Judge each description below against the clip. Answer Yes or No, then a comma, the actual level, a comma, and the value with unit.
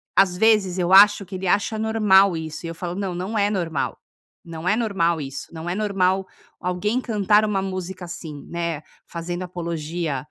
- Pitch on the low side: No, medium, 185 Hz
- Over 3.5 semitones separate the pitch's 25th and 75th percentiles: No, average, 3.0 semitones